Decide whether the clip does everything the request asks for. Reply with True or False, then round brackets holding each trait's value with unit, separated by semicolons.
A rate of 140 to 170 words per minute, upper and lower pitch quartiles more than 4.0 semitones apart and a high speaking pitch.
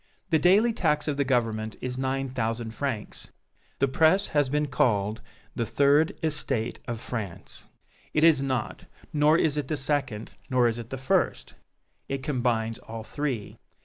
False (160 wpm; 4.5 semitones; 130 Hz)